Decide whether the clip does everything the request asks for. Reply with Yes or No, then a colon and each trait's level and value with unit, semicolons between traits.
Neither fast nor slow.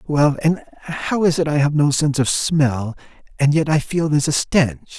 No: fast, 215 wpm